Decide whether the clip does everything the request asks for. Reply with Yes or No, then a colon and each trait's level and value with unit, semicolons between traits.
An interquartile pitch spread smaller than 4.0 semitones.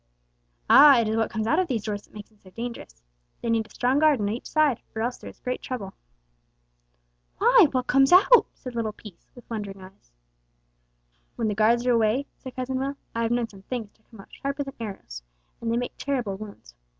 Yes: average, 3.6 semitones